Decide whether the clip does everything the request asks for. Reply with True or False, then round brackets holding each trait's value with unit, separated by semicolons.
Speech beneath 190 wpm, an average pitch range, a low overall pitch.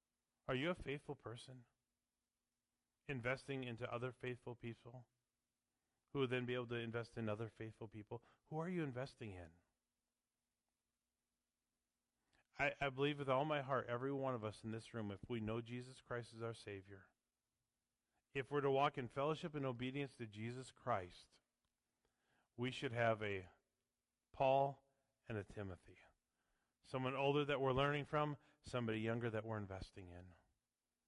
True (155 wpm; 3.6 semitones; 125 Hz)